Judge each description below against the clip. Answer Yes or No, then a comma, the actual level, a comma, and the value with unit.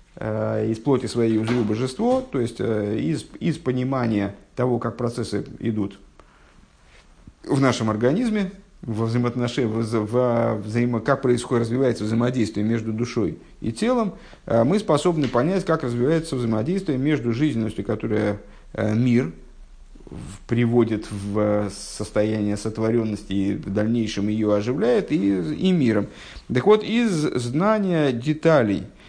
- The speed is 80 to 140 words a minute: Yes, average, 115 wpm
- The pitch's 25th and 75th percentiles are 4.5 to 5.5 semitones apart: No, average, 4.1 semitones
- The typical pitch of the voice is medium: No, low, 115 Hz